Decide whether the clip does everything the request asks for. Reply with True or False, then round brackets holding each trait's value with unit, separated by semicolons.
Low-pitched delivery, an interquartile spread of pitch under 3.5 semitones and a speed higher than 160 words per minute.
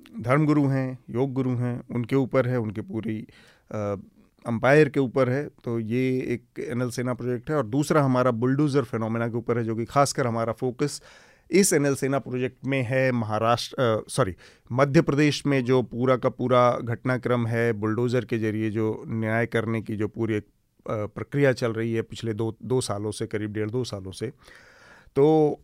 True (125 Hz; 2.9 semitones; 180 wpm)